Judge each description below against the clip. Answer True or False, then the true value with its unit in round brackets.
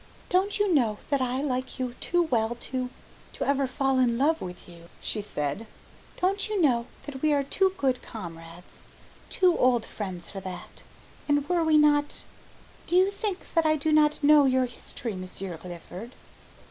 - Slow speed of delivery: False (175 wpm)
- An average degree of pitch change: False (5.8 semitones)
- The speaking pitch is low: False (260 Hz)